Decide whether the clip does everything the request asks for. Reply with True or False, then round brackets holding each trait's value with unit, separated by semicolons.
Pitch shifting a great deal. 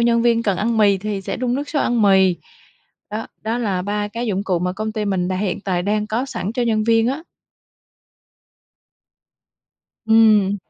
False (3.0 semitones)